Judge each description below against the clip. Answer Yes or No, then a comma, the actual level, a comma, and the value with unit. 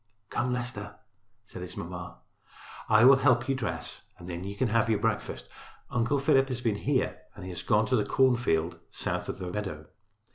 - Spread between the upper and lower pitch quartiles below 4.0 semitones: No, average, 4.6 semitones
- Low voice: Yes, low, 115 Hz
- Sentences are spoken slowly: No, average, 190 wpm